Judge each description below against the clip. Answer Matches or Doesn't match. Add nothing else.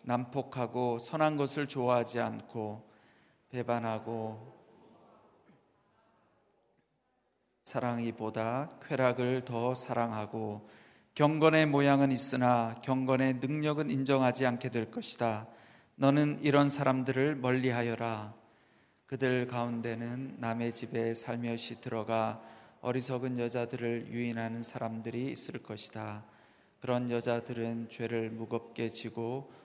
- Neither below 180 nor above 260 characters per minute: Matches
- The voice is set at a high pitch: Doesn't match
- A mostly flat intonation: Matches